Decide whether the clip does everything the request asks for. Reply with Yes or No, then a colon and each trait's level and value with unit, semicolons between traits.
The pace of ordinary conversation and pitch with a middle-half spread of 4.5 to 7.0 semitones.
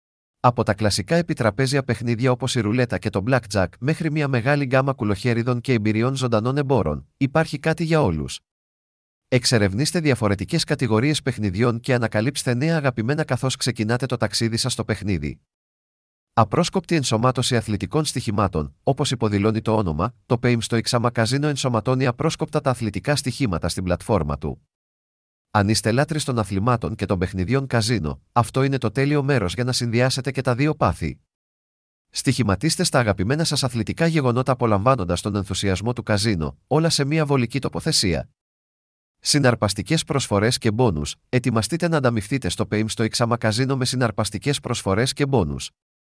Yes: average, 145 wpm; average, 4.8 semitones